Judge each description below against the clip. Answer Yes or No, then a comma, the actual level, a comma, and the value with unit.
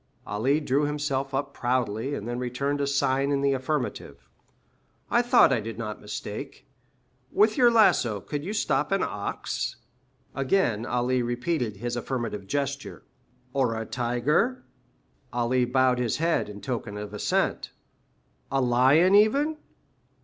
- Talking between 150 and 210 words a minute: No, average, 140 wpm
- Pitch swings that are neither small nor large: Yes, average, 3.4 semitones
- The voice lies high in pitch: No, low, 130 Hz